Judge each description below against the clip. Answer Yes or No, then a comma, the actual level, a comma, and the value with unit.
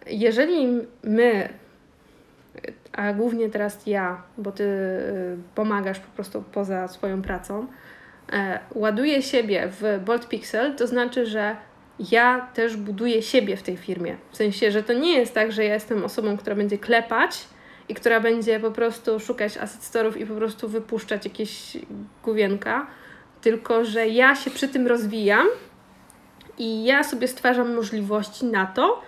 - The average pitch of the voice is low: No, high, 225 Hz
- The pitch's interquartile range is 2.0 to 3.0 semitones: Yes, average, 2.7 semitones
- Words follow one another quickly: No, average, 145 wpm